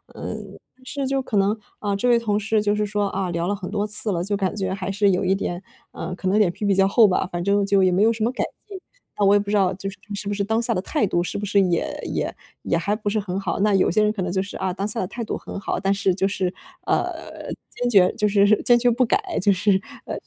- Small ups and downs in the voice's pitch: Yes, narrow, 2.0 semitones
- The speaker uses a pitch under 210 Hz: Yes, high, 200 Hz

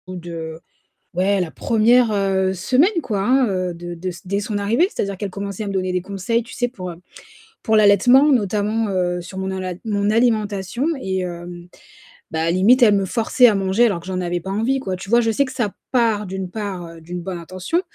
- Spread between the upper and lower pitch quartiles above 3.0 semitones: Yes, average, 3.6 semitones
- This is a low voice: No, high, 200 Hz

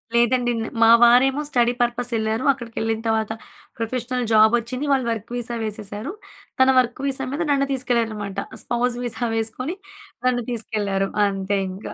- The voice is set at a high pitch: Yes, high, 235 Hz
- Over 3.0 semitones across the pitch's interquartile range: No, narrow, 2.4 semitones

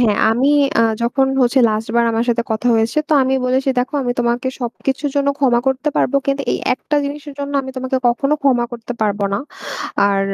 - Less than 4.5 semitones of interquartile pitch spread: Yes, average, 2.9 semitones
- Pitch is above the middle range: Yes, very high, 250 Hz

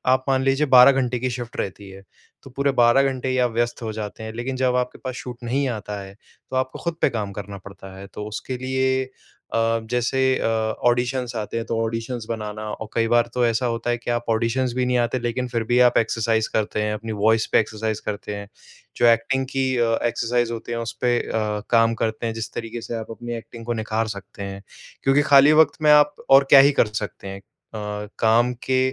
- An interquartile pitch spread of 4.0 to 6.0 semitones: No, narrow, 2.4 semitones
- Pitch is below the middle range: Yes, low, 120 Hz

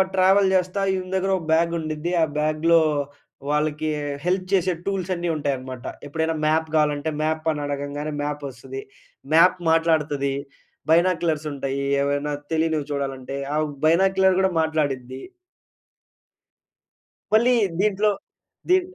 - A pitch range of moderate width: Yes, average, 4.1 semitones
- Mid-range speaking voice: Yes, medium, 160 Hz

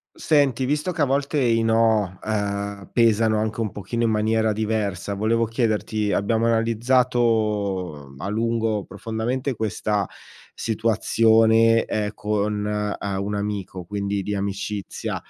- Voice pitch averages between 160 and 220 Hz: No, low, 110 Hz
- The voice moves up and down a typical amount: No, narrow, 2.0 semitones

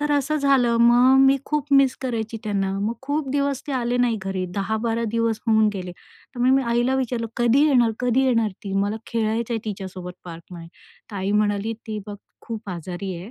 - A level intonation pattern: No, average, 3.9 semitones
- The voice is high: Yes, high, 230 Hz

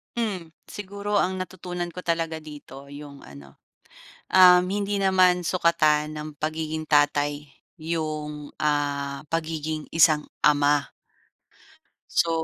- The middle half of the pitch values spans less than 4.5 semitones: Yes, average, 3.3 semitones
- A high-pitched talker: No, medium, 155 Hz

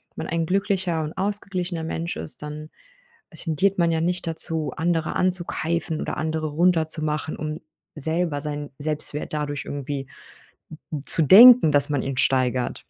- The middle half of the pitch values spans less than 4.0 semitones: Yes, narrow, 2.6 semitones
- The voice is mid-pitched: Yes, medium, 160 Hz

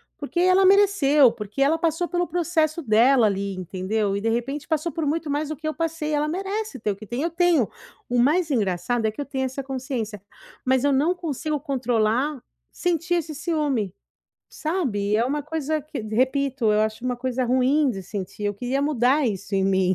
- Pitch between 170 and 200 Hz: No, very high, 275 Hz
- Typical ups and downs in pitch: No, wide, 6.0 semitones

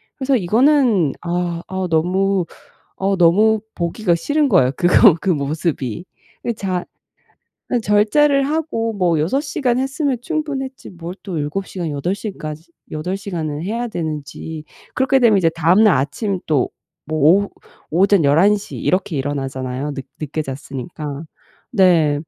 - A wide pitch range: Yes, wide, 5.9 semitones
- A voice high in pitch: No, medium, 180 Hz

